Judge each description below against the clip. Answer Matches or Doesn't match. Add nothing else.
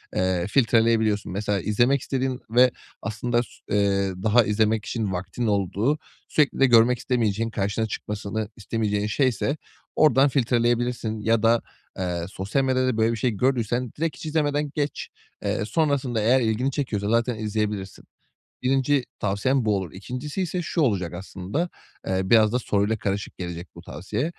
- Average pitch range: Matches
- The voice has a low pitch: Matches